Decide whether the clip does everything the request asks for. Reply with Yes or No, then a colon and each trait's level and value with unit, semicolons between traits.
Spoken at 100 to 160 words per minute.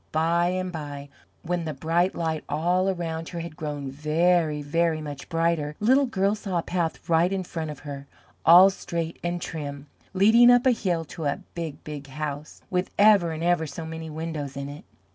No: average, 190 wpm